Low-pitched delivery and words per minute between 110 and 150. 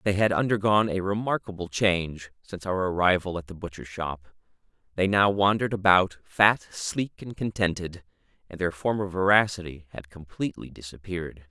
Yes: very low, 95 Hz; average, 145 wpm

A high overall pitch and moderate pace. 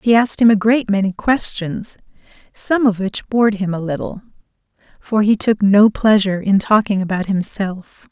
Yes: high, 205 Hz; average, 170 wpm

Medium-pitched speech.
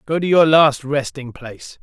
Yes: medium, 145 Hz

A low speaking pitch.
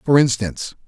Yes: low, 125 Hz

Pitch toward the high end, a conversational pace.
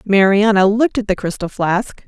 Yes: high, 200 Hz; average, 175 wpm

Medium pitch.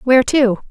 No: very high, 250 Hz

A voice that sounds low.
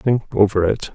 Yes: low, 105 Hz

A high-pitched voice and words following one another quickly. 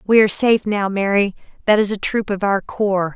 Yes: high, 205 Hz; fast, 230 wpm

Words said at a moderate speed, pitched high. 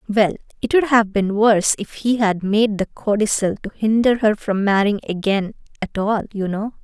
Yes: average, 195 wpm; high, 210 Hz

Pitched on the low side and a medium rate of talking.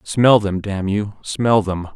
Yes: low, 100 Hz; average, 185 wpm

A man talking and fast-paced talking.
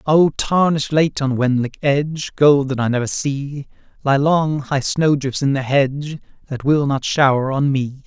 No: male; average, 180 wpm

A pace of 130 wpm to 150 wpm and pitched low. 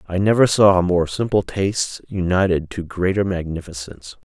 Yes: average, 140 wpm; very low, 90 Hz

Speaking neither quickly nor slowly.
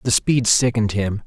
Yes: average, 190 wpm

